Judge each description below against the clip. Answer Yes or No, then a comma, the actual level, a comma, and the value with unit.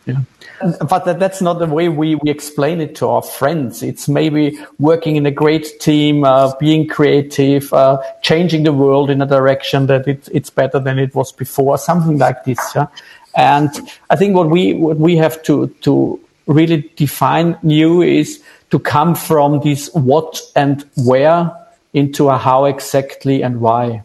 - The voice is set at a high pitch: No, medium, 145 Hz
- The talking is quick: No, average, 175 wpm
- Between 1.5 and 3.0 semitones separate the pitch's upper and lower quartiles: Yes, average, 2.7 semitones